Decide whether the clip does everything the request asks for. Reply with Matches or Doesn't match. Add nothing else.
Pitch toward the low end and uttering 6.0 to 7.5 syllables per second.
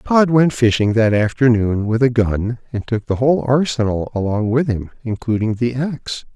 Doesn't match